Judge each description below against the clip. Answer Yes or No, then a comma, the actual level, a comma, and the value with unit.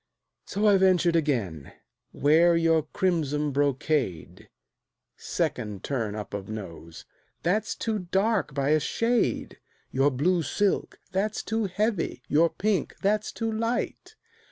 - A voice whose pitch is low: No, medium, 165 Hz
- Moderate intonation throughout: No, wide, 7.0 semitones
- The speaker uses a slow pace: Yes, slow, 125 wpm